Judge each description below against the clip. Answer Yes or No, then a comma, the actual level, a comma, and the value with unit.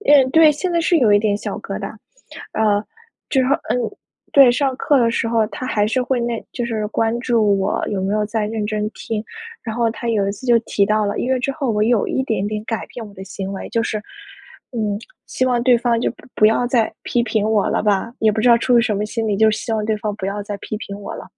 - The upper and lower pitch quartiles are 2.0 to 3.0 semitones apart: Yes, narrow, 2.5 semitones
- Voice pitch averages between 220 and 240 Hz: Yes, high, 225 Hz